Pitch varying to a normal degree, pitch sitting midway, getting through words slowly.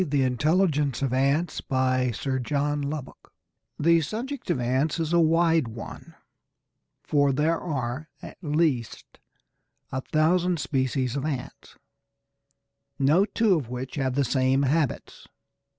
Yes: average, 3.7 semitones; medium, 145 Hz; slow, 130 wpm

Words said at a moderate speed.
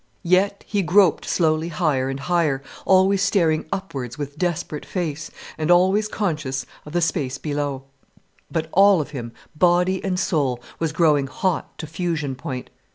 Yes: average, 155 wpm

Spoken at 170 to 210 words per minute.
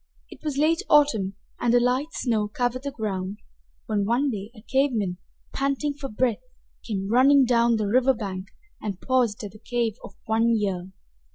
Yes: average, 180 wpm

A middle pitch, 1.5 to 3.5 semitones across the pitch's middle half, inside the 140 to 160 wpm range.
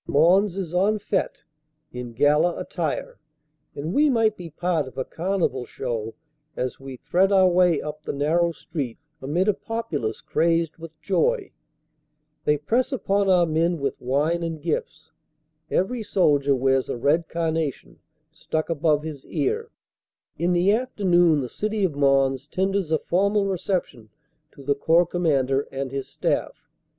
No: medium, 165 Hz; average, 5.1 semitones; average, 150 wpm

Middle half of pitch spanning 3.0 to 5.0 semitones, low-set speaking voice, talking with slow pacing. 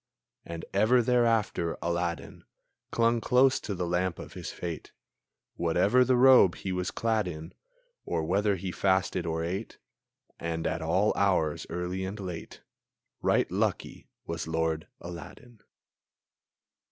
Yes: average, 4.5 semitones; very low, 90 Hz; slow, 130 wpm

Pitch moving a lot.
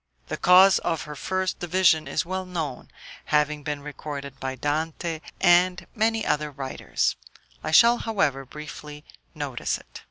No: average, 3.9 semitones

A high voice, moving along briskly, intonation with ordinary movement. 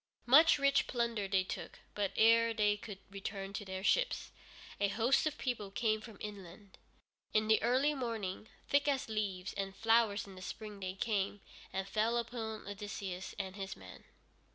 No: high, 210 Hz; average, 170 wpm; average, 3.1 semitones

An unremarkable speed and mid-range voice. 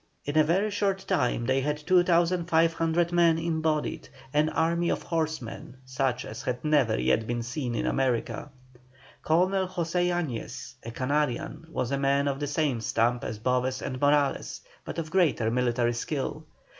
Yes: average, 155 wpm; medium, 150 Hz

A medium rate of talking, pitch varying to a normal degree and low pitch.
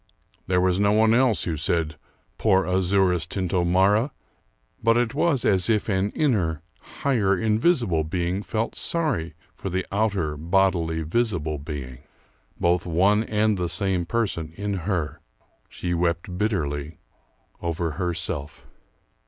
No: slow, 130 wpm; average, 4.2 semitones; very low, 95 Hz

